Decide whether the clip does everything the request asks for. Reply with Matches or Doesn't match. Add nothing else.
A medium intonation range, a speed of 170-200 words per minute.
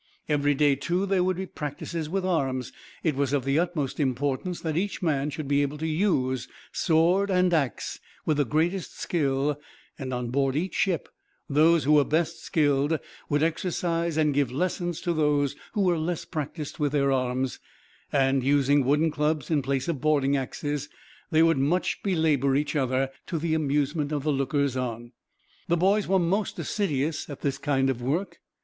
Matches